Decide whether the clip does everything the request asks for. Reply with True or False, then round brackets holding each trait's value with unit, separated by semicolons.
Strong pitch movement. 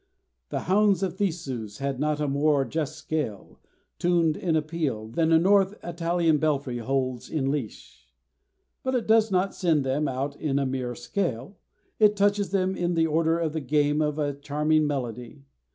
False (4.2 semitones)